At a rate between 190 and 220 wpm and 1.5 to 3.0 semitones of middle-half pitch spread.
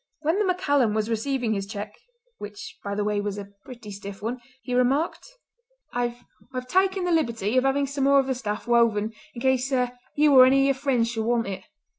No: average, 195 wpm; average, 4.6 semitones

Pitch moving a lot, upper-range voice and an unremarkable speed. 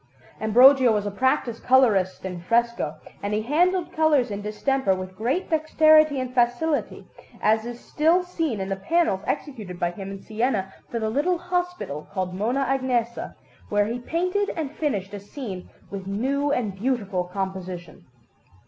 Yes: wide, 6.6 semitones; high, 235 Hz; average, 160 wpm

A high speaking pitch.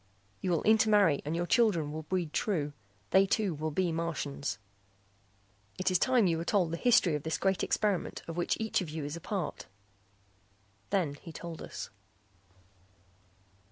No: medium, 170 Hz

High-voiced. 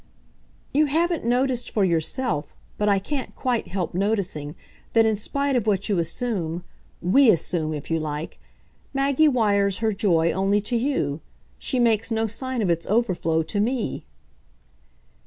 Yes: high, 210 Hz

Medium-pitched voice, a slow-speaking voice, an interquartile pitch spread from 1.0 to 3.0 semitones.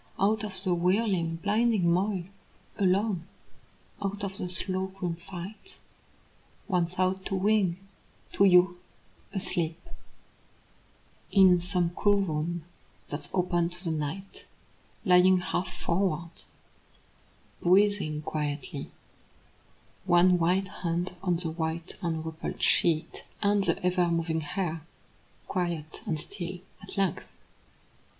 Yes: medium, 180 Hz; slow, 110 wpm; narrow, 2.4 semitones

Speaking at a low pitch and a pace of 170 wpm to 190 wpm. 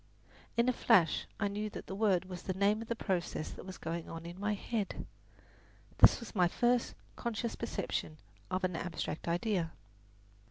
No: high, 190 Hz; average, 175 wpm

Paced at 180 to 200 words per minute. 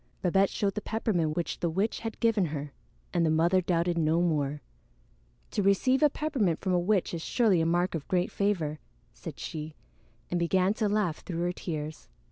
Yes: average, 190 wpm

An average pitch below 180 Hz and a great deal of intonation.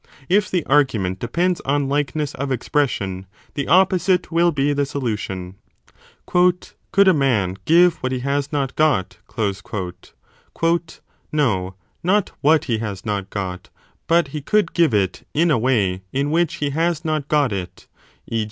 Yes: medium, 140 Hz; wide, 7.4 semitones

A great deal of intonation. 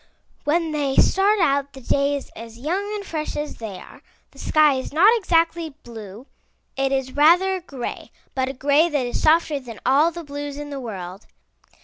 No: average, 4.1 semitones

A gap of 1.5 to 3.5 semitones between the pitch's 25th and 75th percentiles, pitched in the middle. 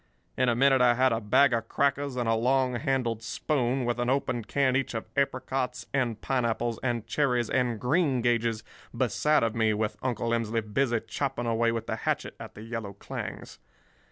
No: narrow, 2.4 semitones; low, 120 Hz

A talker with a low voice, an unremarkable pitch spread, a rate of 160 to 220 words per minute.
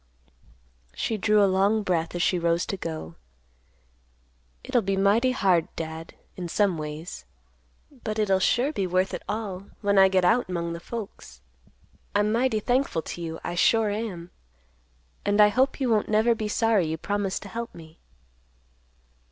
No: high, 195 Hz; average, 4.2 semitones; average, 165 wpm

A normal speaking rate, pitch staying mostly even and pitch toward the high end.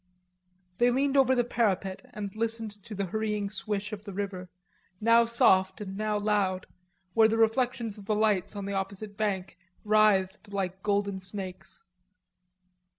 Yes: average, 150 wpm; narrow, 2.3 semitones; high, 210 Hz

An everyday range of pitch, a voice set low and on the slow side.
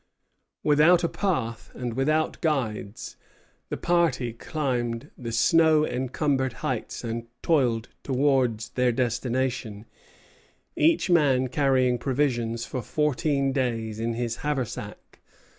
Yes: average, 4.0 semitones; low, 130 Hz; slow, 110 wpm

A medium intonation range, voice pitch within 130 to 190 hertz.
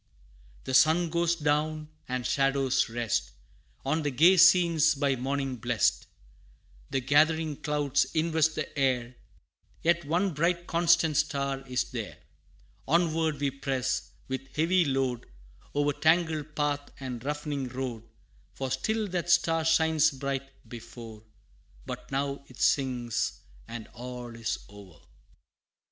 Yes: average, 3.7 semitones; medium, 140 Hz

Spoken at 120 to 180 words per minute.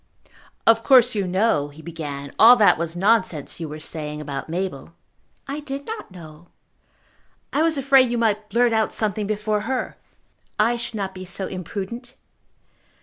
Yes: average, 160 wpm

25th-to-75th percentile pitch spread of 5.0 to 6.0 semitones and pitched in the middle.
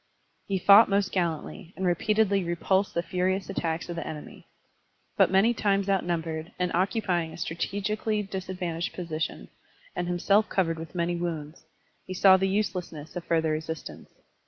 No: average, 2.8 semitones; medium, 180 Hz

